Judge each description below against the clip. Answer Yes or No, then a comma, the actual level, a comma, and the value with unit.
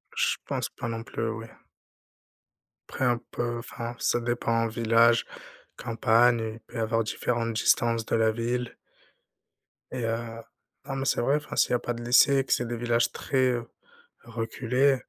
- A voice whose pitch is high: No, low, 120 Hz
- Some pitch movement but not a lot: No, narrow, 1.1 semitones